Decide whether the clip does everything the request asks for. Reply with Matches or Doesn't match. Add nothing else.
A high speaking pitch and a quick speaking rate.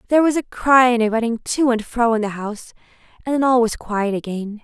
Matches